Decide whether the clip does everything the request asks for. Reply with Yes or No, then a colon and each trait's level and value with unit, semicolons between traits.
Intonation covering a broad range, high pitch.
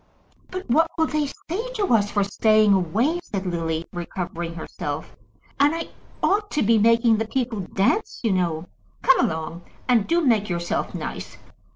Yes: wide, 8.9 semitones; high, 215 Hz